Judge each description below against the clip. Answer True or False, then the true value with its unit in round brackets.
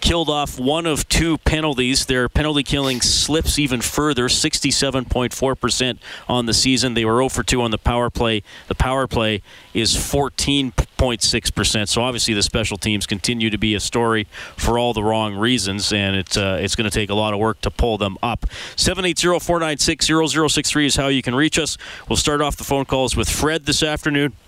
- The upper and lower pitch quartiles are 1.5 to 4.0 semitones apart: False (4.7 semitones)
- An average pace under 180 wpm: False (195 wpm)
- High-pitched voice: False (125 Hz)